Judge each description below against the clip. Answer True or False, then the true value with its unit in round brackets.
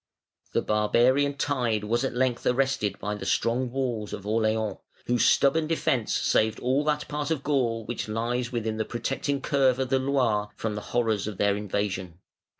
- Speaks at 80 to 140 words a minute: False (175 wpm)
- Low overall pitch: True (120 Hz)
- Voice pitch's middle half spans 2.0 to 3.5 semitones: False (3.9 semitones)